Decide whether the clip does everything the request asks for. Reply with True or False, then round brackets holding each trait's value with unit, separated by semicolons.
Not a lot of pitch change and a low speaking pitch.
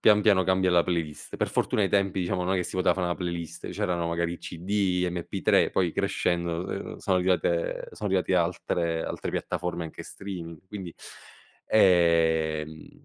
True (1.9 semitones; 90 Hz)